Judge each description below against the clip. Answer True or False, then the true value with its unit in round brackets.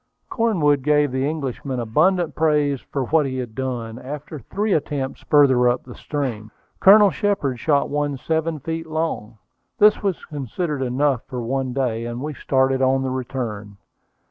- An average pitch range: True (3.5 semitones)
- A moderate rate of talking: True (160 wpm)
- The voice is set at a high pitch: False (135 Hz)